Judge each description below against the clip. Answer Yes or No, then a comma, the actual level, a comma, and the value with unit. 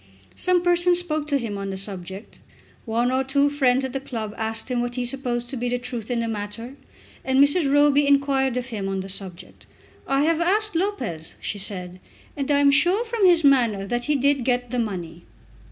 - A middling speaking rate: No, fast, 210 wpm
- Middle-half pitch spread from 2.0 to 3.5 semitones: No, average, 4.5 semitones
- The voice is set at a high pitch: Yes, very high, 255 Hz